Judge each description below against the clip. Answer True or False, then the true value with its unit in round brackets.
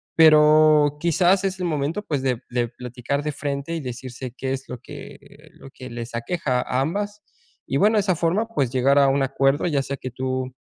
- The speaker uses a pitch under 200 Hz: True (140 Hz)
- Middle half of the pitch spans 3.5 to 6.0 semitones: True (4.2 semitones)